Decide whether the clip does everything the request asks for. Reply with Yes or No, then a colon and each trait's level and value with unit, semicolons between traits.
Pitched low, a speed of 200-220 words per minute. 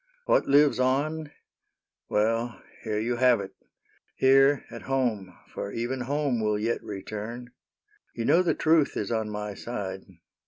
No: low, 120 Hz; average, 160 wpm